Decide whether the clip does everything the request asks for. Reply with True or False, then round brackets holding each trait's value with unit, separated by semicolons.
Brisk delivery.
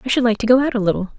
True (405 wpm)